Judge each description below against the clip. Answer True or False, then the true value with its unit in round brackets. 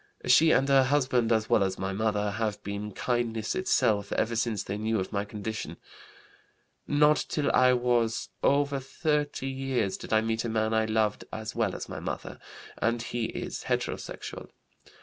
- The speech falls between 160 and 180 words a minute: True (170 wpm)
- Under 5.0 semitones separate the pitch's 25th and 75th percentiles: True (3.5 semitones)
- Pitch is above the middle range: False (115 Hz)